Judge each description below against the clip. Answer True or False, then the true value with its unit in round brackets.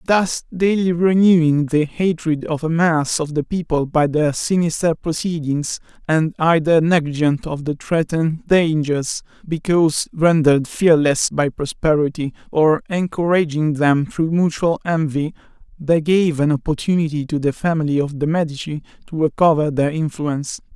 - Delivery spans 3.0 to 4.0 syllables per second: False (4.6 syllables/s)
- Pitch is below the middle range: False (155 Hz)